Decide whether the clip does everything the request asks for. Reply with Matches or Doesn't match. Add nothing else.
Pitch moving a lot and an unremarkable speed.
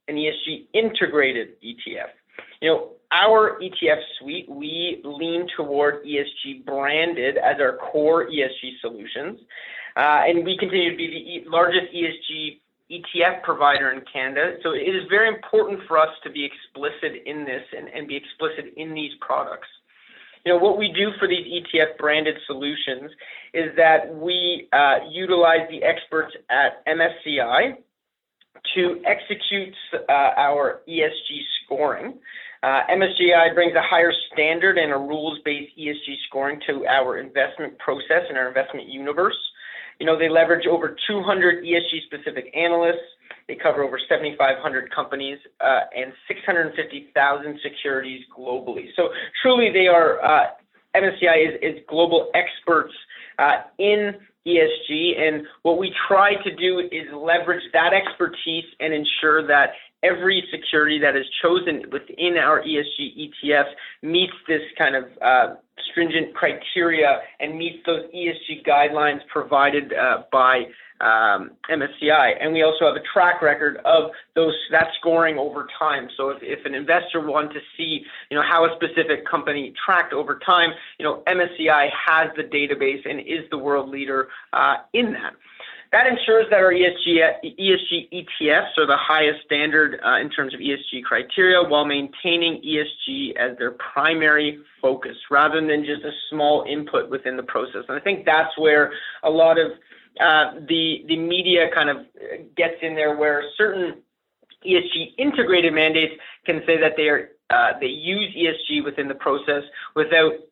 Doesn't match